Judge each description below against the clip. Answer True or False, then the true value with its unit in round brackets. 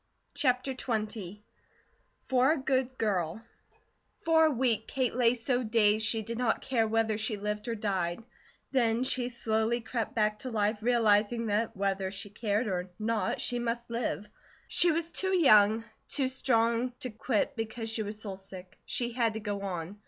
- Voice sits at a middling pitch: False (225 Hz)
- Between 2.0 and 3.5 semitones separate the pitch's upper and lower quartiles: True (2.9 semitones)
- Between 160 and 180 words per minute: True (170 wpm)